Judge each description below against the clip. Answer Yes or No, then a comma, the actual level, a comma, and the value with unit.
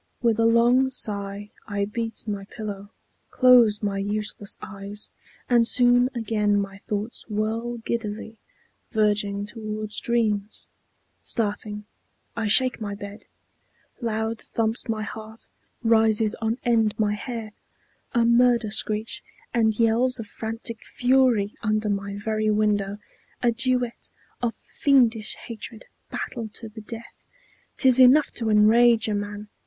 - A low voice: No, high, 220 Hz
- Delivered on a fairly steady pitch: Yes, narrow, 2.1 semitones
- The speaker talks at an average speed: No, slow, 130 wpm